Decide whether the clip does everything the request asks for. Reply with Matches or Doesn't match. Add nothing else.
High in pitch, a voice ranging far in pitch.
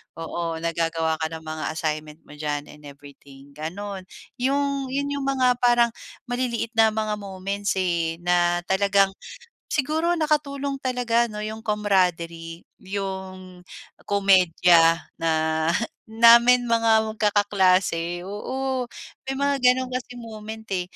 Matches